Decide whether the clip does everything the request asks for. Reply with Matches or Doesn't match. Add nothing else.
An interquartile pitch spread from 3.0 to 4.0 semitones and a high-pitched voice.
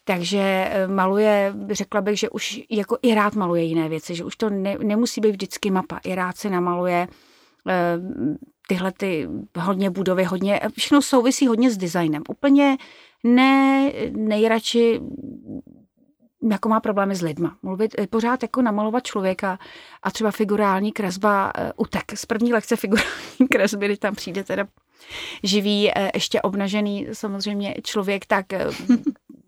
Matches